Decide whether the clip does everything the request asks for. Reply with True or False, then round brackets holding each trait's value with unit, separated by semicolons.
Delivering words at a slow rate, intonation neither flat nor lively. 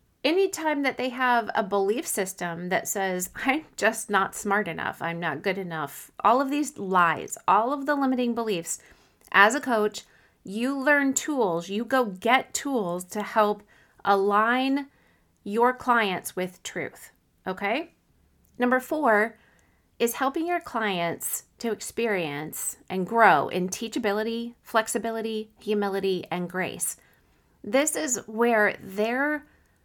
True (130 wpm; 4.9 semitones)